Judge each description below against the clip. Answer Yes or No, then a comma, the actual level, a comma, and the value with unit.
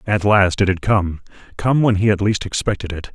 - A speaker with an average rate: No, fast, 210 wpm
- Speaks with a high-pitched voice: No, low, 100 Hz